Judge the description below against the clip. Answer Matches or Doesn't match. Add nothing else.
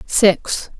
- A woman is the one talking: Matches